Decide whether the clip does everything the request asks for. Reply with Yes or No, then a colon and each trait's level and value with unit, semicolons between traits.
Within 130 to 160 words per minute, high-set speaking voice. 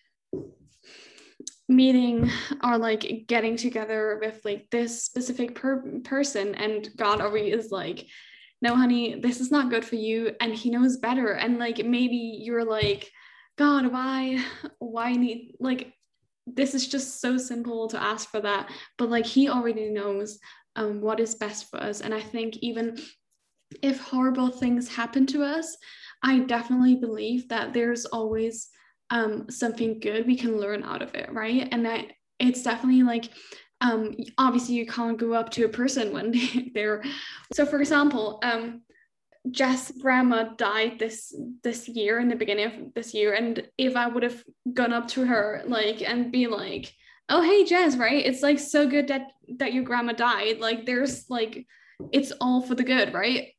No: average, 170 wpm; high, 240 Hz